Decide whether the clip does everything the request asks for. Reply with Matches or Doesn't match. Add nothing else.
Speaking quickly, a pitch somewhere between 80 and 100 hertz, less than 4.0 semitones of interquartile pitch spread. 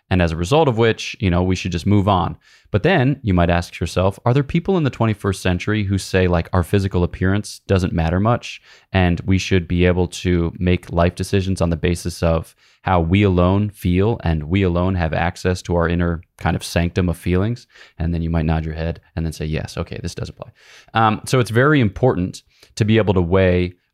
Matches